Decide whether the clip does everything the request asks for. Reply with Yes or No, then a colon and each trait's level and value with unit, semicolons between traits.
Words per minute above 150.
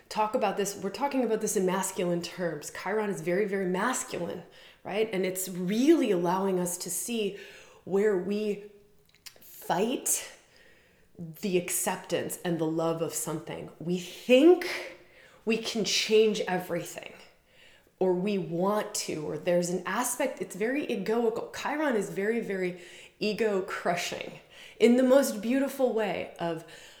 No: slow, 135 wpm